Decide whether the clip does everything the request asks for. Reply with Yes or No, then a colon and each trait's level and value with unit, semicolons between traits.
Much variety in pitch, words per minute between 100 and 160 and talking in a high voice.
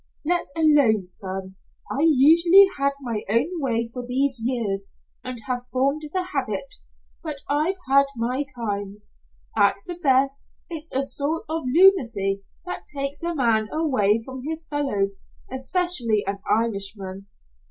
Yes: wide, 6.1 semitones; average, 140 wpm; very high, 260 Hz